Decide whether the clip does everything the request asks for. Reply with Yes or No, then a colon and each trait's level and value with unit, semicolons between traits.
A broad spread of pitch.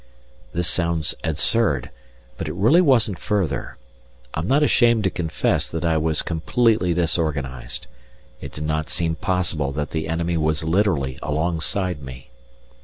No: average, 3.3 semitones